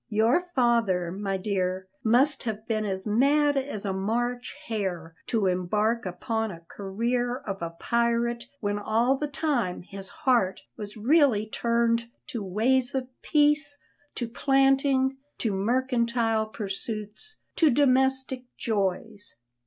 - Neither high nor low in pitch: No, high, 230 Hz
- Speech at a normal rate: No, slow, 130 wpm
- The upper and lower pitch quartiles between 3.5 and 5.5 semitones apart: Yes, average, 4.2 semitones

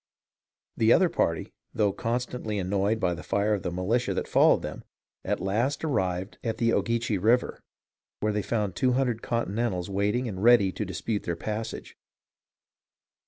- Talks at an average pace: Yes, average, 160 wpm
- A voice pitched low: Yes, low, 105 Hz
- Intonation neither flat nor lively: Yes, average, 3.6 semitones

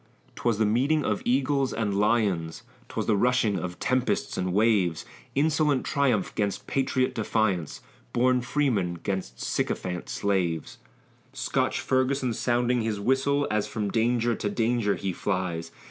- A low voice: Yes, low, 110 Hz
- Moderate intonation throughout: Yes, average, 4.6 semitones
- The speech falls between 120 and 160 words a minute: Yes, slow, 135 wpm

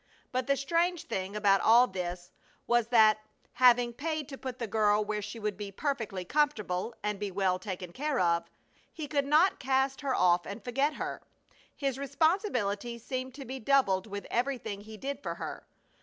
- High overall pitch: Yes, high, 235 Hz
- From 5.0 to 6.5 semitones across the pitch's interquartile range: Yes, wide, 5.4 semitones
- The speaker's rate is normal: Yes, average, 180 wpm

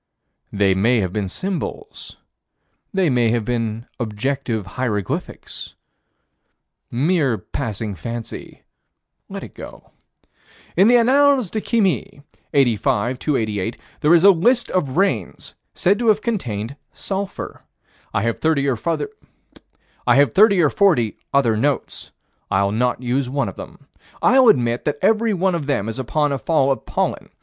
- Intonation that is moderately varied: No, wide, 8.5 semitones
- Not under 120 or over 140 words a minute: Yes, slow, 135 wpm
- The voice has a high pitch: No, medium, 140 Hz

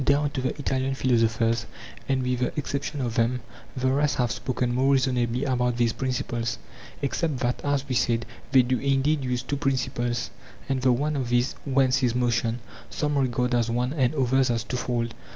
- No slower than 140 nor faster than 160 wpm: No, average, 185 wpm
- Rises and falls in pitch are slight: Yes, narrow, 2.0 semitones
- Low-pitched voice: Yes, low, 125 Hz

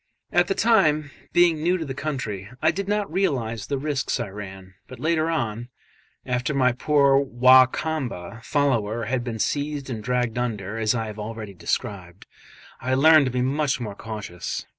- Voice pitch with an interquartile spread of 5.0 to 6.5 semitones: Yes, average, 5.3 semitones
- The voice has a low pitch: Yes, low, 130 Hz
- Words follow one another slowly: No, average, 175 wpm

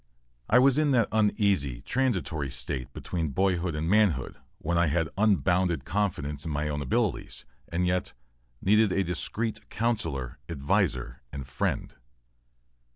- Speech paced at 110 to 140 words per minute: Yes, slow, 135 wpm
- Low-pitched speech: Yes, very low, 85 Hz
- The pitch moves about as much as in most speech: No, wide, 6.3 semitones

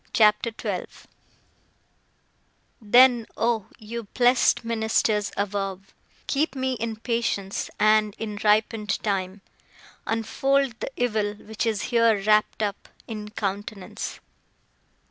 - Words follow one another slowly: Yes, slow, 105 wpm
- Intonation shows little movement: Yes, narrow, 2.1 semitones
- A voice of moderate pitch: No, high, 215 Hz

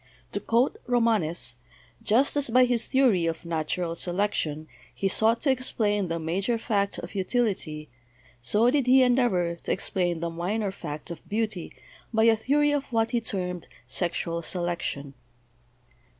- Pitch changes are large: Yes, wide, 5.7 semitones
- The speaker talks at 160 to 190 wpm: No, average, 150 wpm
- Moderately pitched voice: No, high, 200 Hz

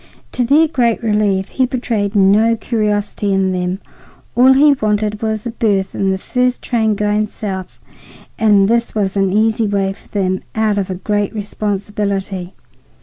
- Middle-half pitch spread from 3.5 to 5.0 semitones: No, narrow, 2.5 semitones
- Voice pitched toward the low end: No, high, 210 Hz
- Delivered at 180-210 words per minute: No, average, 160 wpm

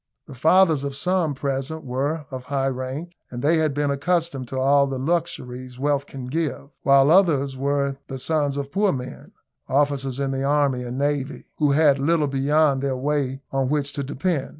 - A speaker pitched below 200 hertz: Yes, medium, 140 Hz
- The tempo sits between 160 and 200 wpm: Yes, average, 185 wpm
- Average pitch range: No, narrow, 1.9 semitones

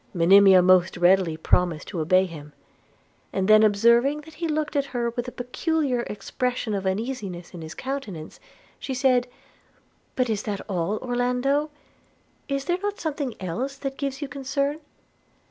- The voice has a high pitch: Yes, high, 240 Hz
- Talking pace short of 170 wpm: Yes, average, 160 wpm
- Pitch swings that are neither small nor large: No, wide, 6.6 semitones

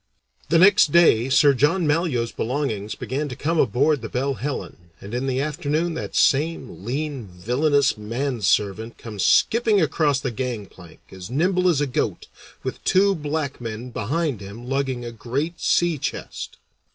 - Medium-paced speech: Yes, average, 155 wpm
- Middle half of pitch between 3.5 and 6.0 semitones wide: Yes, average, 4.9 semitones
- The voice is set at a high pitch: No, low, 135 Hz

